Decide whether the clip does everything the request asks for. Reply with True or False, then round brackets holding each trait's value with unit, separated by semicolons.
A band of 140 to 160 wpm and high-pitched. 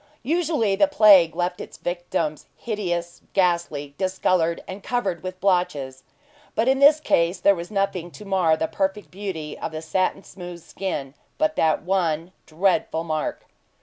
False (150 wpm; 180 Hz)